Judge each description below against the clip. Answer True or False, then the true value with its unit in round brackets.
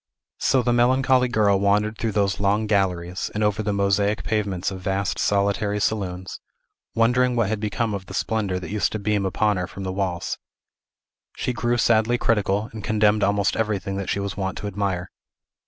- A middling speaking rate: True (185 wpm)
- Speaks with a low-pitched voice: True (105 Hz)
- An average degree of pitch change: False (2.0 semitones)